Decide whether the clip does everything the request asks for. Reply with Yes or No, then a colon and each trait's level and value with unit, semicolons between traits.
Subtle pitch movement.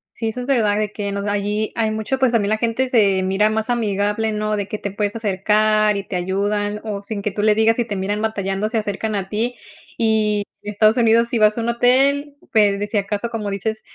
Yes: narrow, 1.7 semitones